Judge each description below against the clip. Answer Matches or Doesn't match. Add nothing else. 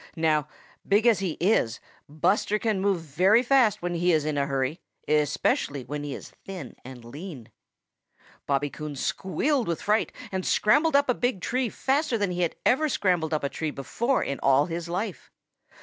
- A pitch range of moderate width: Doesn't match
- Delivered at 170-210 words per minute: Matches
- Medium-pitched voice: Matches